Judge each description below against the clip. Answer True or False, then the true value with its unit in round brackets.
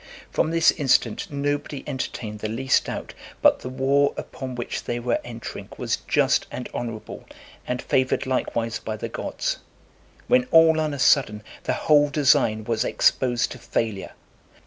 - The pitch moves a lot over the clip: False (3.9 semitones)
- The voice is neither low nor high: False (130 Hz)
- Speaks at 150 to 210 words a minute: True (155 wpm)